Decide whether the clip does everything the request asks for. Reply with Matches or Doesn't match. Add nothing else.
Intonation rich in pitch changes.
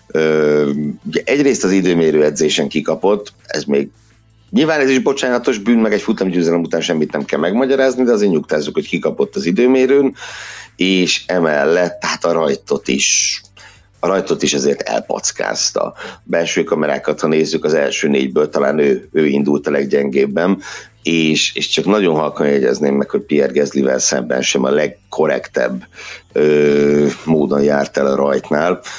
Matches